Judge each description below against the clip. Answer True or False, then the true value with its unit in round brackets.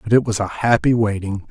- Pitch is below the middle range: True (110 Hz)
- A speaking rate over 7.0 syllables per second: False (5.5 syllables/s)